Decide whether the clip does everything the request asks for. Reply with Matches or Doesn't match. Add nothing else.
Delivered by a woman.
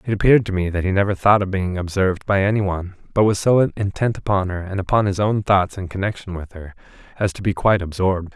Doesn't match